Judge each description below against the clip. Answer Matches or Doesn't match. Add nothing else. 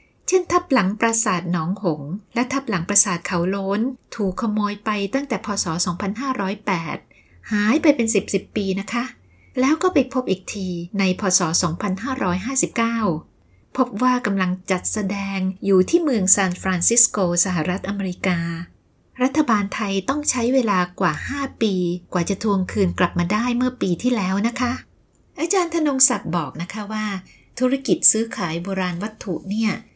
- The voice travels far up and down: Doesn't match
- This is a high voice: Matches